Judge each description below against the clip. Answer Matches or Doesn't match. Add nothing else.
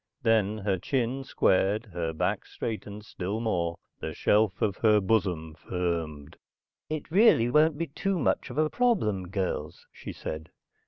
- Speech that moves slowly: Doesn't match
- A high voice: Doesn't match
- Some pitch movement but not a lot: Doesn't match